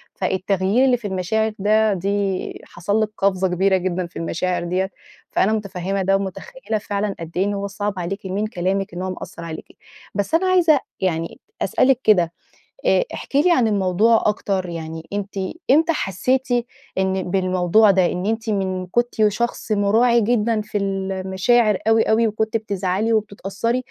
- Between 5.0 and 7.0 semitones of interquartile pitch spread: No, average, 2.9 semitones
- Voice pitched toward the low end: No, high, 200 Hz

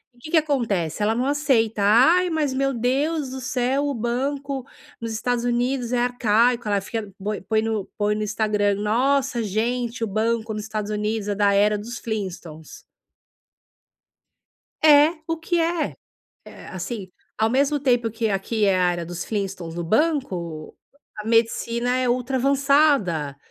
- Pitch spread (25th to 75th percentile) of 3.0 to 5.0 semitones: Yes, average, 4.3 semitones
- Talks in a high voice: Yes, high, 230 Hz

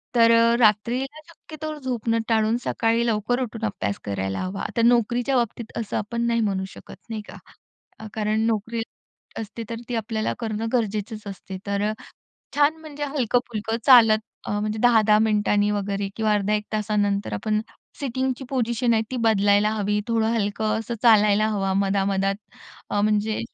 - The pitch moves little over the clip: Yes, narrow, 2.2 semitones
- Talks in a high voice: Yes, high, 220 Hz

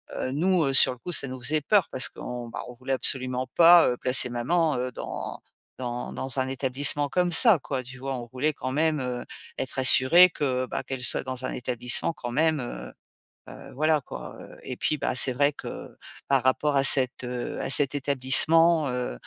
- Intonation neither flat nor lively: Yes, average, 3.1 semitones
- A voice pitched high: No, low, 130 Hz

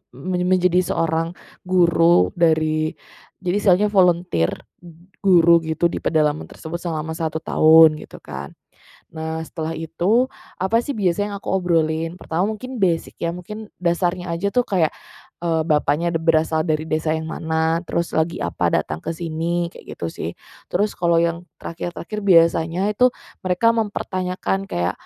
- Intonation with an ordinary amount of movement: No, narrow, 2.3 semitones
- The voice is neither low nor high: Yes, medium, 170 Hz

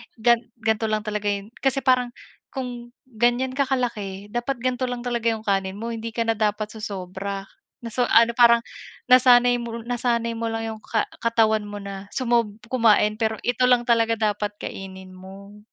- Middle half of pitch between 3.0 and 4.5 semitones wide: No, narrow, 2.6 semitones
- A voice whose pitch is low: No, high, 230 Hz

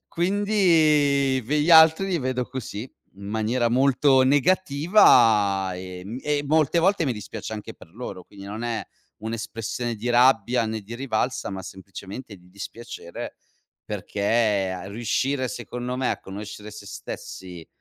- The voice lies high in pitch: No, low, 120 Hz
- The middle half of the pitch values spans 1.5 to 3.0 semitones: No, wide, 5.4 semitones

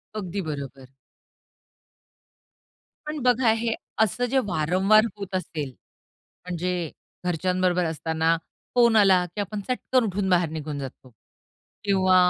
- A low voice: No, medium, 185 Hz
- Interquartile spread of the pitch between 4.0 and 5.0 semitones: Yes, average, 4.4 semitones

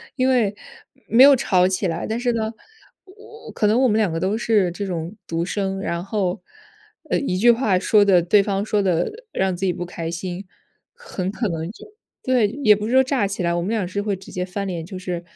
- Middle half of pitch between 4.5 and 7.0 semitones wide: No, average, 3.6 semitones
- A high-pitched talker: Yes, high, 200 Hz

